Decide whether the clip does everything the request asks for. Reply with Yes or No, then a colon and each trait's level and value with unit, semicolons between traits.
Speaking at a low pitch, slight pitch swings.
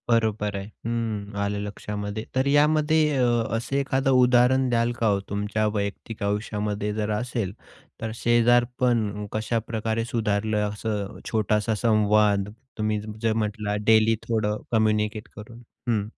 Yes: low, 110 Hz; narrow, 2.2 semitones